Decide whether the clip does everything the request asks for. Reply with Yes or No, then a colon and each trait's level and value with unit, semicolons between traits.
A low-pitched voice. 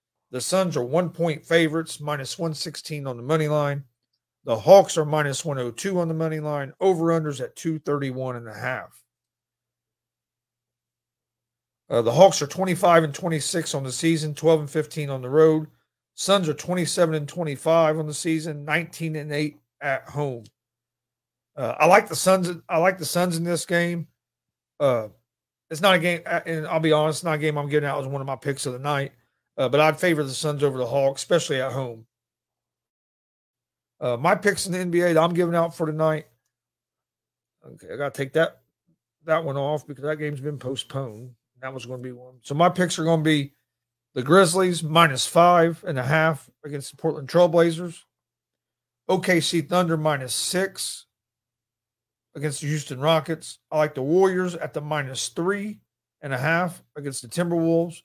No: medium, 155 Hz